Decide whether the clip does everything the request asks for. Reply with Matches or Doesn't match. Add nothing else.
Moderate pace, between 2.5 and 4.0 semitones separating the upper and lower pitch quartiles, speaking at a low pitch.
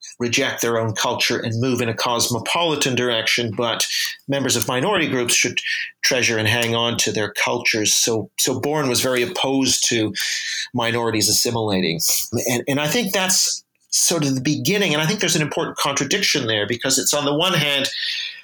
Doesn't match